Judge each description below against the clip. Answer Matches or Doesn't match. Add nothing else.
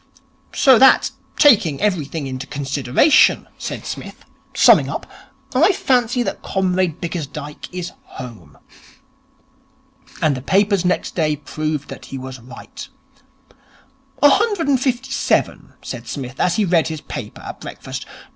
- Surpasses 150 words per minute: Doesn't match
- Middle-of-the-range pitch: Matches